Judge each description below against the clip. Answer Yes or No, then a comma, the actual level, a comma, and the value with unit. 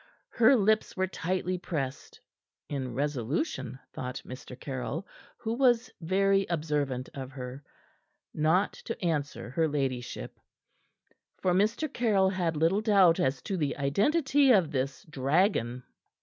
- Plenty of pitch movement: Yes, wide, 6.5 semitones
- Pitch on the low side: No, medium, 165 Hz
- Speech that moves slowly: Yes, slow, 125 wpm